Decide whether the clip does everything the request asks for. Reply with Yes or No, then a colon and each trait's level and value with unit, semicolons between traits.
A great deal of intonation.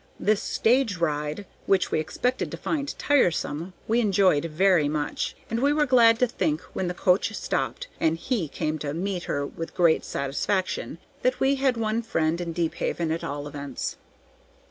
Yes: wide, 6.5 semitones